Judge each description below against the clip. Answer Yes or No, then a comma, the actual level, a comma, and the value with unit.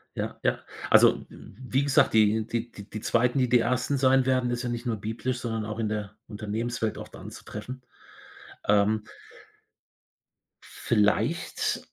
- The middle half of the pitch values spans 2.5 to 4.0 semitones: Yes, average, 2.8 semitones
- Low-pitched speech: Yes, low, 115 Hz